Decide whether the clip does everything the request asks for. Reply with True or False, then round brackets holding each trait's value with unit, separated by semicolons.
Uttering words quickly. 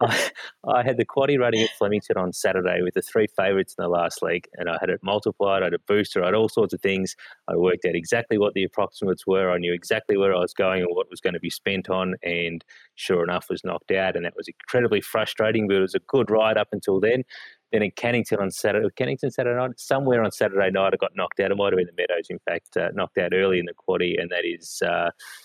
True (260 wpm)